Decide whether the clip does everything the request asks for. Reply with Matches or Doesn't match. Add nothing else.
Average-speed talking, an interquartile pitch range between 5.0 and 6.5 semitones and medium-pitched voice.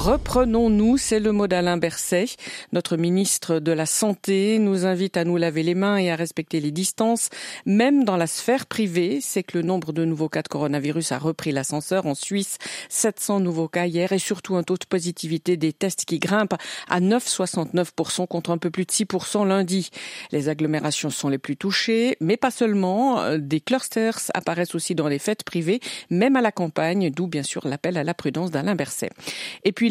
Doesn't match